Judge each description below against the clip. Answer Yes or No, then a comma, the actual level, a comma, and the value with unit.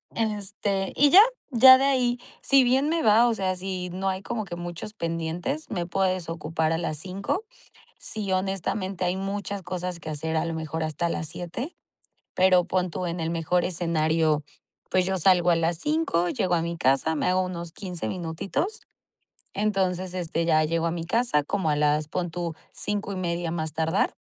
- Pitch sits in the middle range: Yes, medium, 180 Hz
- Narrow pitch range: No, average, 3.1 semitones